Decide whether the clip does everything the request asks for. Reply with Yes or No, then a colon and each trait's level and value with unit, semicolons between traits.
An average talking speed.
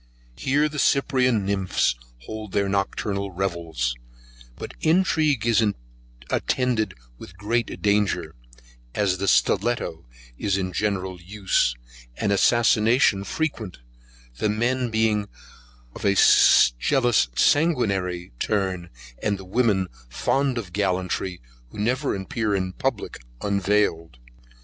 No: slow, 110 wpm